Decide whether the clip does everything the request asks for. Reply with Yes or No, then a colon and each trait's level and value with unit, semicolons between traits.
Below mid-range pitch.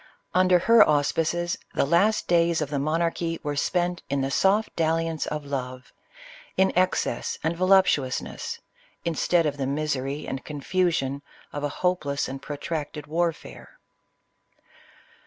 No: medium, 160 Hz